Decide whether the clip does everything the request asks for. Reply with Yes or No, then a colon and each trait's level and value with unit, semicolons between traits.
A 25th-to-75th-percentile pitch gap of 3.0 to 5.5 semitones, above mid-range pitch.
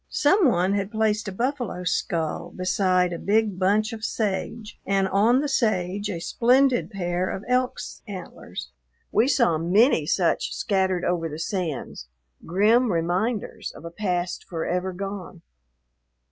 Yes: average, 3.7 semitones; high, 195 Hz